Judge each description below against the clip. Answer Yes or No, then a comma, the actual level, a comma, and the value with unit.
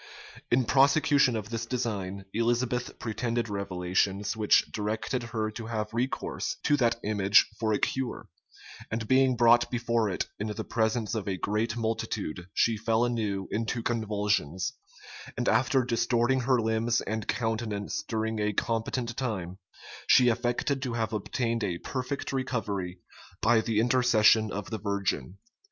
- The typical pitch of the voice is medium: No, low, 115 Hz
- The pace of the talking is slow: No, average, 145 wpm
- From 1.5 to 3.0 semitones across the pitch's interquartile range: Yes, narrow, 2.4 semitones